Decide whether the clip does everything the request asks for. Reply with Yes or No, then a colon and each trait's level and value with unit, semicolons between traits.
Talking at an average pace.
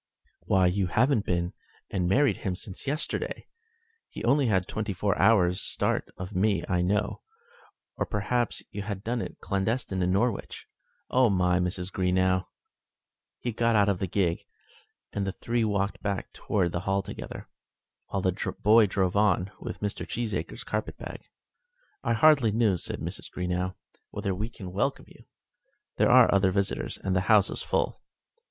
Yes: average, 160 wpm